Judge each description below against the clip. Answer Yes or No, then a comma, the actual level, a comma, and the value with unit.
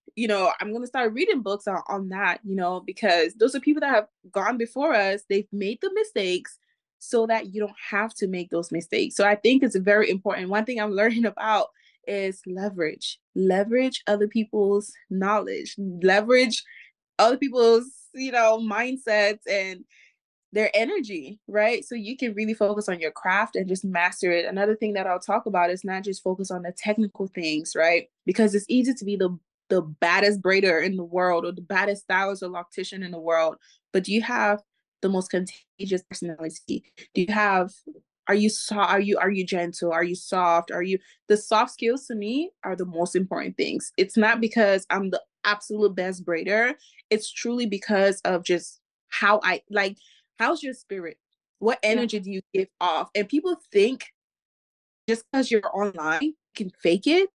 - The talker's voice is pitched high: Yes, high, 205 Hz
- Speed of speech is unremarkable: Yes, average, 190 wpm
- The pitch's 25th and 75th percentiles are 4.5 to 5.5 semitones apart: No, average, 3.6 semitones